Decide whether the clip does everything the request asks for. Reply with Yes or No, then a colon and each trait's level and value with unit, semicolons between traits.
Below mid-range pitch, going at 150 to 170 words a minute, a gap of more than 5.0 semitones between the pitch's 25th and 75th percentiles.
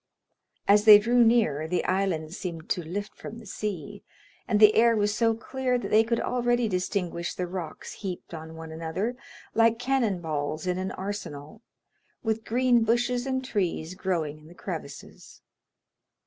No: high, 200 Hz; average, 160 wpm; wide, 5.5 semitones